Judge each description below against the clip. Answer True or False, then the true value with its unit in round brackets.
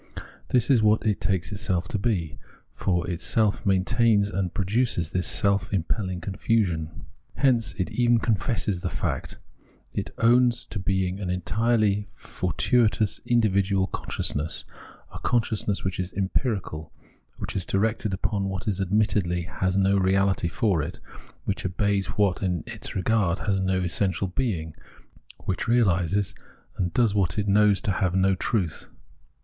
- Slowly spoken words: False (145 wpm)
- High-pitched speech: False (100 Hz)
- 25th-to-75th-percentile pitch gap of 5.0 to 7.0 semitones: False (2.8 semitones)